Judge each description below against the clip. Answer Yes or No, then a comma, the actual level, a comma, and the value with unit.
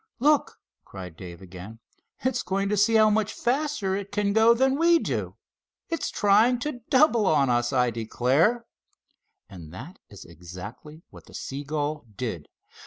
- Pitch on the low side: No, medium, 185 Hz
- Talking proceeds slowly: No, average, 155 wpm